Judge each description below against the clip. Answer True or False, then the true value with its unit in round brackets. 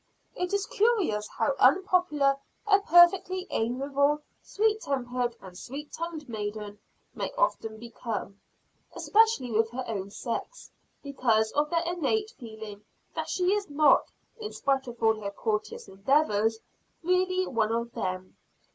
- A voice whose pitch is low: False (270 Hz)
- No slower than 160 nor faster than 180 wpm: False (135 wpm)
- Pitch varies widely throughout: True (8.4 semitones)